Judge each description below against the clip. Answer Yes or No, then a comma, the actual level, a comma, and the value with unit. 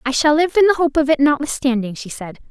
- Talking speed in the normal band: No, fast, 265 wpm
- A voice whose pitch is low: No, very high, 280 Hz